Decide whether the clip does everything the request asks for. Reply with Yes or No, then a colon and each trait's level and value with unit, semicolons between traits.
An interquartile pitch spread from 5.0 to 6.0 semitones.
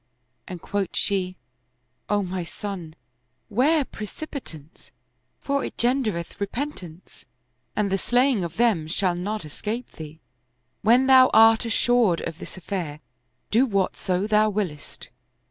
Yes: wide, 5.5 semitones